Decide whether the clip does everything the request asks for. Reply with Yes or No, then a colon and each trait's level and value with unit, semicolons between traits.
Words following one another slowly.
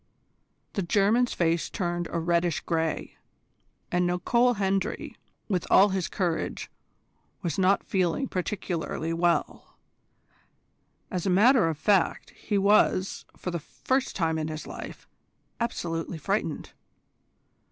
Yes: slow, 120 wpm